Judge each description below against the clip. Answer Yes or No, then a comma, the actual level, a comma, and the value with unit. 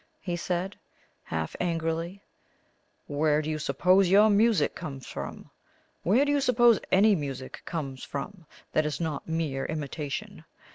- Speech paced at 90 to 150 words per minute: Yes, average, 140 wpm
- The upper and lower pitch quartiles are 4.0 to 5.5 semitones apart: Yes, average, 5.1 semitones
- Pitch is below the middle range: No, medium, 165 Hz